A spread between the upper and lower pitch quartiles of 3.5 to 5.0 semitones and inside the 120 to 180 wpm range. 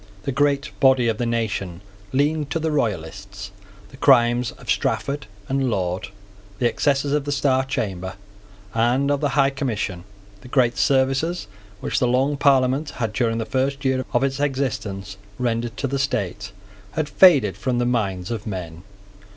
Yes: average, 4.5 semitones; average, 165 wpm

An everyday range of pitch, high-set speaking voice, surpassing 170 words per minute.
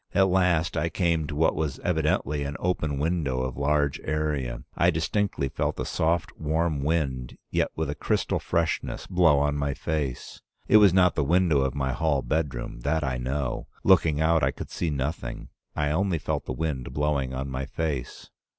No: average, 3.1 semitones; very low, 75 Hz; average, 185 wpm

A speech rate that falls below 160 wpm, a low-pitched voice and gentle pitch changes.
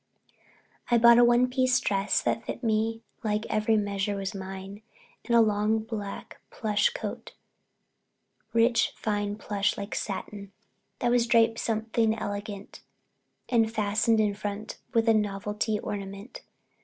No: average, 140 wpm; high, 215 Hz; narrow, 2.0 semitones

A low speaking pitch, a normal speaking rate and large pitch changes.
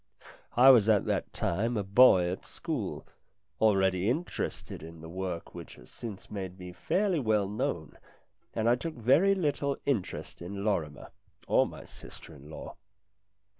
Yes: low, 100 Hz; average, 155 wpm; wide, 5.8 semitones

